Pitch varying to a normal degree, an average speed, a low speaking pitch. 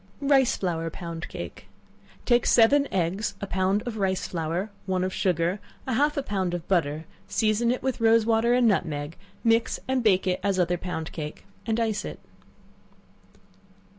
No: average, 4.6 semitones; average, 165 wpm; high, 195 Hz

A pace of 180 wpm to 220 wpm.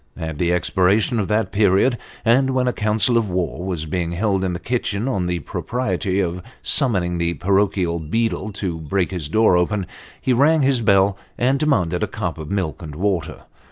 Yes: average, 190 wpm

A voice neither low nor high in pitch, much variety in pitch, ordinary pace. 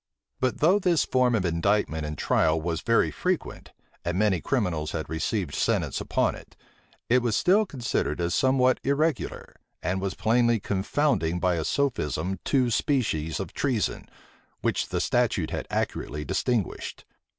No: low, 105 Hz; wide, 7.5 semitones; average, 150 wpm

